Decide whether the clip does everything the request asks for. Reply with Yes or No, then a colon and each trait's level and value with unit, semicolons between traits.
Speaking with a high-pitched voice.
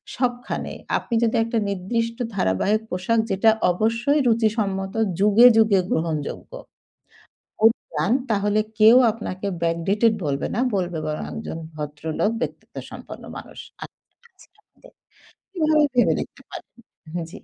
Yes: high, 205 Hz